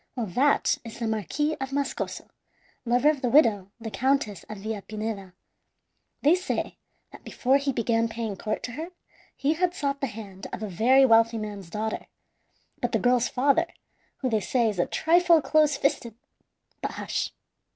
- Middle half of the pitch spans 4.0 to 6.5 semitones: Yes, average, 4.5 semitones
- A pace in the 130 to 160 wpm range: No, average, 170 wpm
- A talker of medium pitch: No, high, 235 Hz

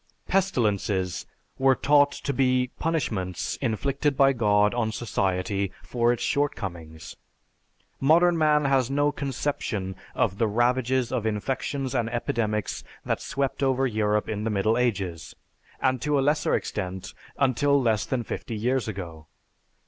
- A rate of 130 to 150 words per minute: Yes, slow, 135 wpm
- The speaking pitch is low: Yes, low, 120 Hz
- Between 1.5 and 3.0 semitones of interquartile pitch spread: No, average, 4.7 semitones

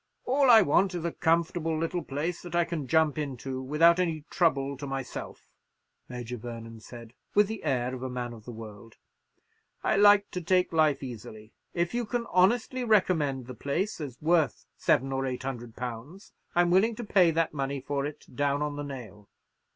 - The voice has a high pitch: No, medium, 150 Hz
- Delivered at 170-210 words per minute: Yes, average, 190 wpm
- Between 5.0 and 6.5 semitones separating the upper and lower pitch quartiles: Yes, wide, 5.5 semitones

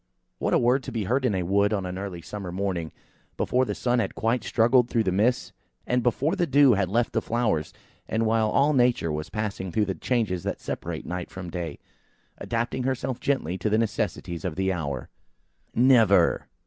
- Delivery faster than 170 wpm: Yes, average, 200 wpm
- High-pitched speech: No, low, 110 Hz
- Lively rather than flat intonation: No, average, 5.0 semitones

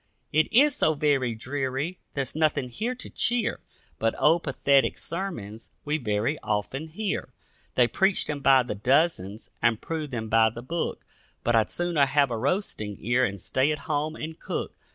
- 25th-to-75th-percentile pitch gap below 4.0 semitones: No, wide, 5.4 semitones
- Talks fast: No, average, 175 wpm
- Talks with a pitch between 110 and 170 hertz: Yes, medium, 140 Hz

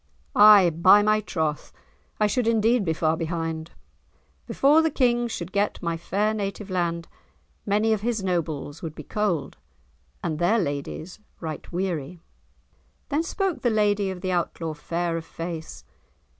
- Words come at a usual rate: Yes, average, 150 wpm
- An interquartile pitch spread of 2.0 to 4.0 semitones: No, average, 4.4 semitones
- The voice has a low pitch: No, medium, 185 Hz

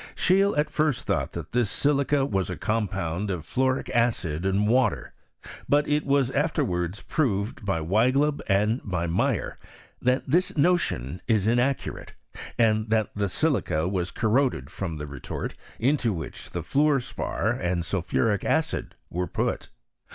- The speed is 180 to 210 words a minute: No, average, 145 wpm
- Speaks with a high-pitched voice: No, low, 110 Hz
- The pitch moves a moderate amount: No, wide, 7.1 semitones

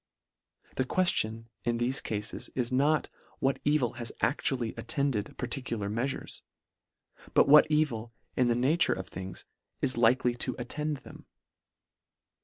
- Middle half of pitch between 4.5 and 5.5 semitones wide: No, average, 3.2 semitones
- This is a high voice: No, low, 125 Hz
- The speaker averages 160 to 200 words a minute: No, average, 140 wpm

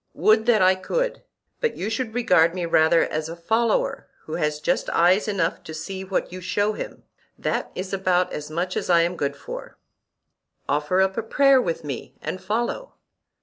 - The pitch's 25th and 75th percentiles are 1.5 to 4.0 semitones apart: No, average, 4.5 semitones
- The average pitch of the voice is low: No, medium, 185 Hz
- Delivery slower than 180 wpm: No, average, 185 wpm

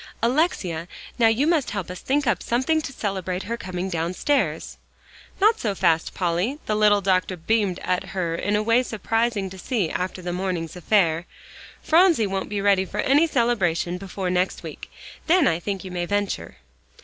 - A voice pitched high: Yes, high, 195 Hz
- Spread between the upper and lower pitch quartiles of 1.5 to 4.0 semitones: No, average, 4.6 semitones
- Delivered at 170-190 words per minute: Yes, average, 175 wpm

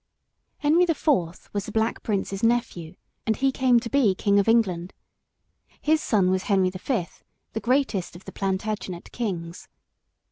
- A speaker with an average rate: Yes, average, 170 wpm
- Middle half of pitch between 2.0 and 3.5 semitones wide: No, average, 4.5 semitones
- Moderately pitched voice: No, high, 210 Hz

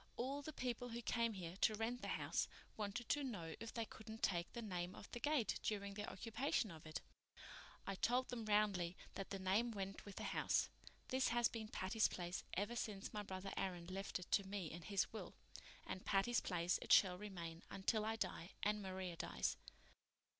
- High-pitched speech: Yes, high, 205 Hz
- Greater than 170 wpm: Yes, average, 195 wpm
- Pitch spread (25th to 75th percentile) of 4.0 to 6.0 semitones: No, average, 3.5 semitones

